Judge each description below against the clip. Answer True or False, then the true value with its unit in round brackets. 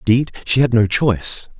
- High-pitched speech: False (120 Hz)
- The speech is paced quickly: False (190 wpm)